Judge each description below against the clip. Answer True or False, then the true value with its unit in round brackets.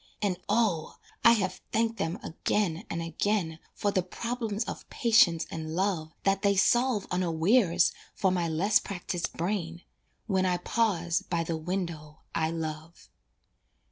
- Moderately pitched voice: True (180 Hz)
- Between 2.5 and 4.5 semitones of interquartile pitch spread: True (3.7 semitones)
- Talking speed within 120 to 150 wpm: True (140 wpm)